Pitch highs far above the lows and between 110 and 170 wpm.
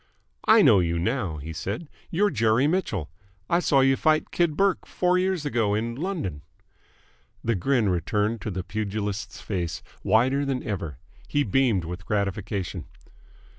Yes: wide, 6.8 semitones; average, 150 wpm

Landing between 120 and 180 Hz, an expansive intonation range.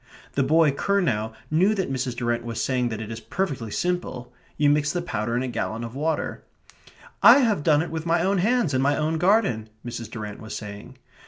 Yes: medium, 140 Hz; wide, 6.5 semitones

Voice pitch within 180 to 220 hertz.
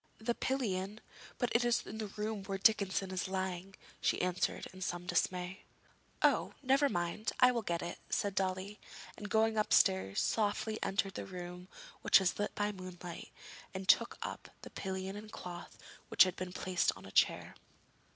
Yes: high, 190 Hz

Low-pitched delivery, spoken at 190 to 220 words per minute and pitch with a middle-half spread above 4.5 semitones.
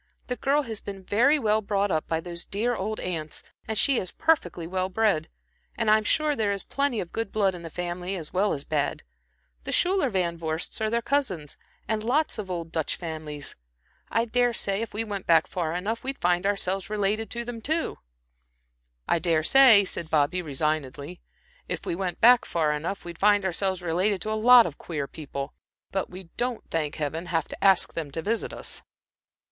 No: high, 190 Hz; average, 200 wpm; average, 5.0 semitones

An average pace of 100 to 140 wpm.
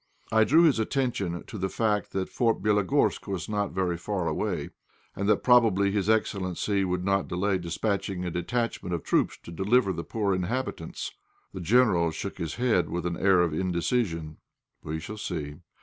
No: average, 175 wpm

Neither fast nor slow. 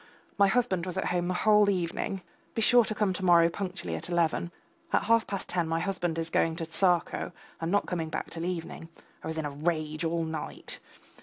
No: fast, 215 wpm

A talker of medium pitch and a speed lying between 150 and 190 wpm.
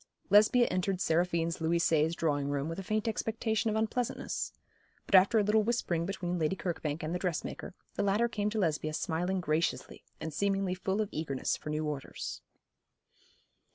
Yes: medium, 180 Hz; average, 170 wpm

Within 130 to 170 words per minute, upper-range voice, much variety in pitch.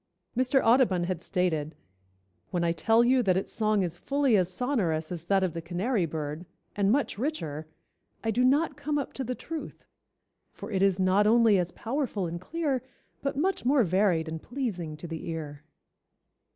No: average, 180 wpm; high, 195 Hz; wide, 6.8 semitones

